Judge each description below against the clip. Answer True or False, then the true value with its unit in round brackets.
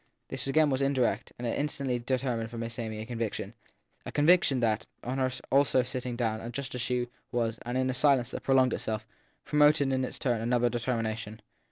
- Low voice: True (125 Hz)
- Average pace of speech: True (195 wpm)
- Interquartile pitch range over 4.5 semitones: False (2.5 semitones)